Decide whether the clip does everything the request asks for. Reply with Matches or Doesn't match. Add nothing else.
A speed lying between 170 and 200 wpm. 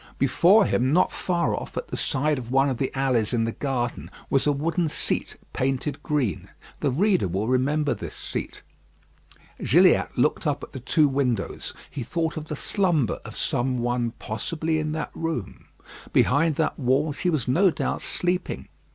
Matches